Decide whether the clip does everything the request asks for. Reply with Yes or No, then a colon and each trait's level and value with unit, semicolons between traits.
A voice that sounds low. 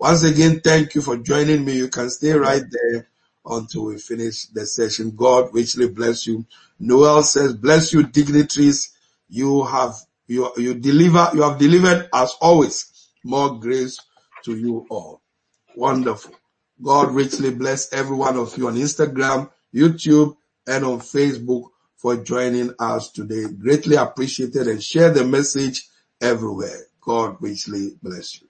Yes: low, 130 Hz